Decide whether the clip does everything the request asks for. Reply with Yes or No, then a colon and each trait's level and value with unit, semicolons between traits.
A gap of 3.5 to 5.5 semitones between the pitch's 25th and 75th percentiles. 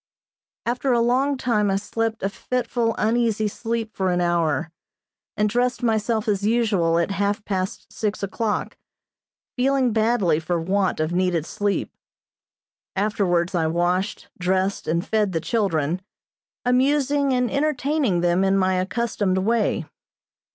Yes: average, 4.4 semitones